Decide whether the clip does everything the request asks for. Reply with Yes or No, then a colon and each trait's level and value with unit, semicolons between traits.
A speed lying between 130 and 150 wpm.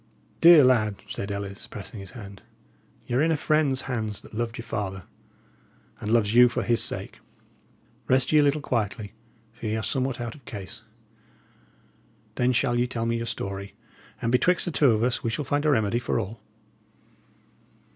No: average, 185 wpm